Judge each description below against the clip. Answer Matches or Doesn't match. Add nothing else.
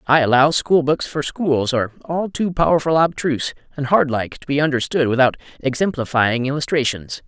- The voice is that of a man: Matches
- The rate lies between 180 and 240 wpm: Doesn't match